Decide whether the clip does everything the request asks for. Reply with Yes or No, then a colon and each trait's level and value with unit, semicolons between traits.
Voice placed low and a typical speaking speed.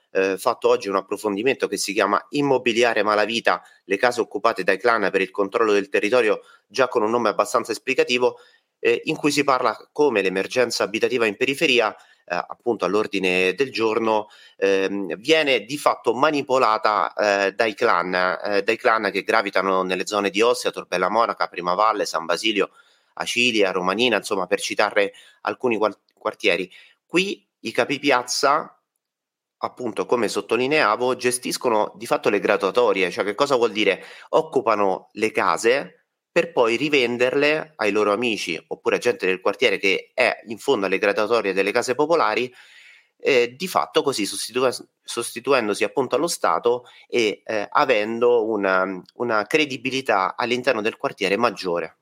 Yes: low, 125 Hz; average, 150 wpm